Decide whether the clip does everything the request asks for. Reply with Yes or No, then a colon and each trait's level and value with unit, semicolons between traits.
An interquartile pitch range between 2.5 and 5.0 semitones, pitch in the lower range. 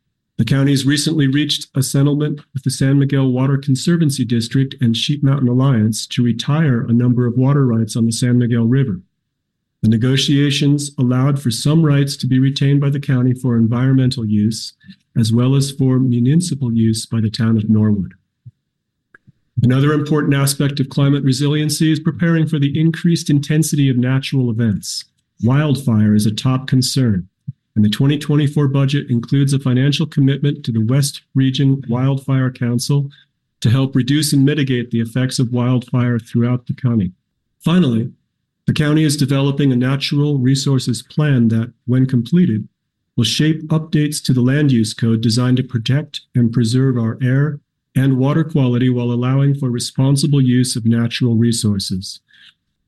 Yes: average, 3.0 semitones; low, 130 Hz